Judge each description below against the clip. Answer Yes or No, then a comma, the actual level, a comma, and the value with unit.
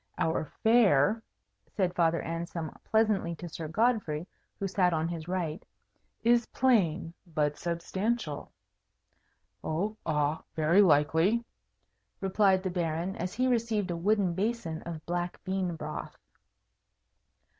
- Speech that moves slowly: Yes, slow, 120 wpm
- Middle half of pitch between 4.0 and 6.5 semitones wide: Yes, average, 4.3 semitones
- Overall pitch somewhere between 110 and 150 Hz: No, medium, 175 Hz